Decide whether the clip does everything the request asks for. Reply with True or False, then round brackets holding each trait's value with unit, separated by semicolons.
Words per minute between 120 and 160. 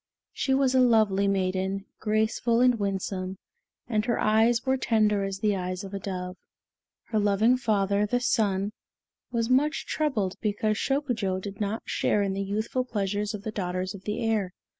False (170 wpm)